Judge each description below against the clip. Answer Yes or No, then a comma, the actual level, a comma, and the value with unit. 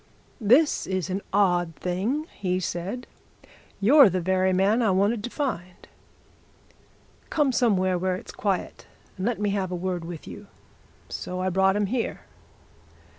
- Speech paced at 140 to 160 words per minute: Yes, average, 150 wpm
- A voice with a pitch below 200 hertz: Yes, high, 190 Hz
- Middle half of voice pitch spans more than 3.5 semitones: No, average, 3.2 semitones